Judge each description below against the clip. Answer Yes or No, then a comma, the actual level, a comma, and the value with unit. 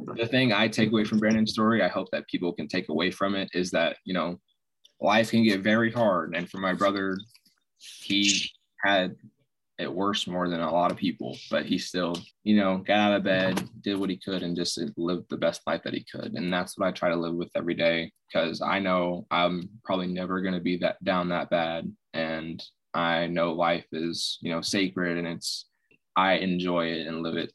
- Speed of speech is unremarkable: No, fast, 220 wpm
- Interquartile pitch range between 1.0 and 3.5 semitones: Yes, average, 2.8 semitones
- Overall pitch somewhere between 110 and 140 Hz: No, very low, 90 Hz